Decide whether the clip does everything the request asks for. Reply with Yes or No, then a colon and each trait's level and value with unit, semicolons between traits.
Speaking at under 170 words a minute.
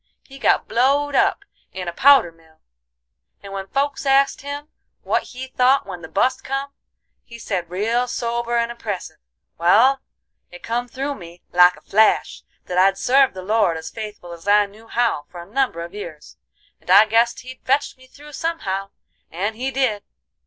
No: average, 180 wpm